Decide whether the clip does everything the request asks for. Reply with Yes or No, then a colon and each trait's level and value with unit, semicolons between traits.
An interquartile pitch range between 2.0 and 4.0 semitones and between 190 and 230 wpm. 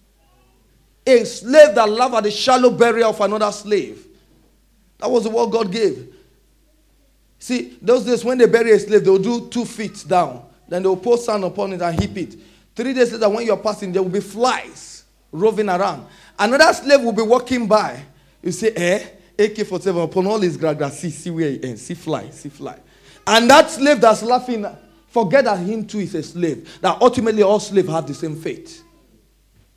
No: average, 4.4 semitones; average, 195 wpm